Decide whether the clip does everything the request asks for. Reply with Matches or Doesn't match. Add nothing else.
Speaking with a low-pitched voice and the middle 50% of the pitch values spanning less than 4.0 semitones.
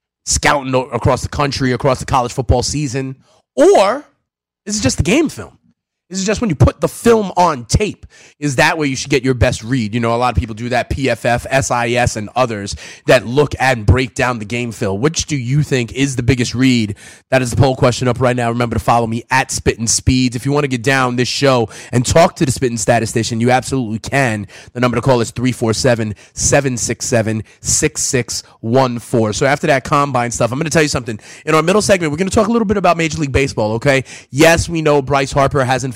Matches